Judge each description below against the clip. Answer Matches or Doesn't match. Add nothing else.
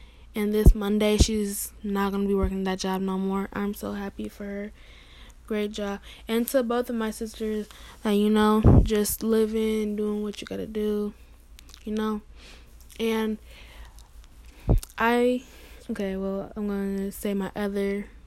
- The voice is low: Doesn't match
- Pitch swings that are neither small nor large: Doesn't match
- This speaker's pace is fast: Doesn't match